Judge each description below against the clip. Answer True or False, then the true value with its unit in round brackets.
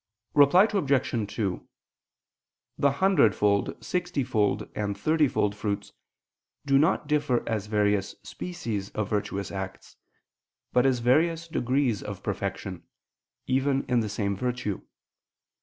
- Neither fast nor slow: False (110 wpm)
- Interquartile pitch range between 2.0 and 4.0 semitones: False (5.6 semitones)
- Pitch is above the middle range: False (120 Hz)